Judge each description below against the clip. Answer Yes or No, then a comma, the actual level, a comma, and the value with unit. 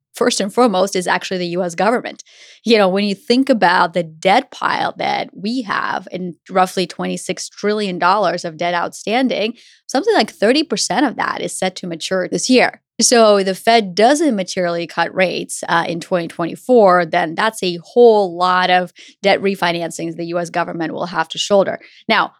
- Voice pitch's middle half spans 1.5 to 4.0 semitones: Yes, average, 3.4 semitones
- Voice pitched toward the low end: No, medium, 185 Hz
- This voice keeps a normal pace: Yes, average, 175 wpm